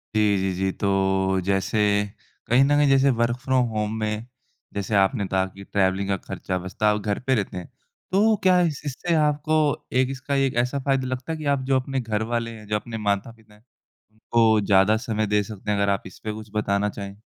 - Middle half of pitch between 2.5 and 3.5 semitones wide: No, average, 4.6 semitones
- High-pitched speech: No, low, 110 Hz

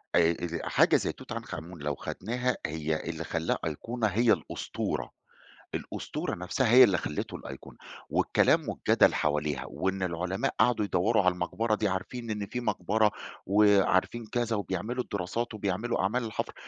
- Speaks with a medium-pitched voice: No, low, 100 Hz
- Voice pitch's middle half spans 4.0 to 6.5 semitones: Yes, average, 4.6 semitones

